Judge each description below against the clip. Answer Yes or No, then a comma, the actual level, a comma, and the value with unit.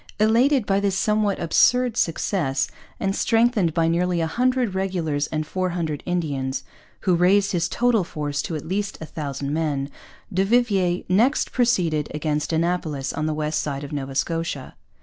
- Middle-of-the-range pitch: Yes, medium, 170 Hz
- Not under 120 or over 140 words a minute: No, average, 165 wpm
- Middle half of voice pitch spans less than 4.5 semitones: No, average, 4.9 semitones